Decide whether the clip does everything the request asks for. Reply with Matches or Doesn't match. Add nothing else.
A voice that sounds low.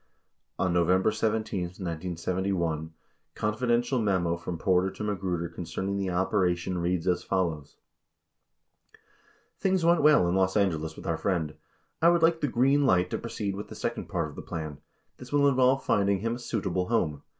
Matches